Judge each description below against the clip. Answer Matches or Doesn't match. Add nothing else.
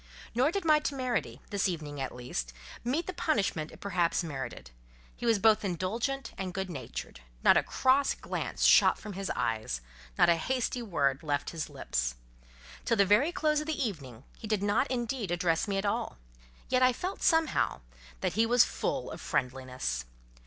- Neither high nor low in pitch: Doesn't match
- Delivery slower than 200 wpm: Matches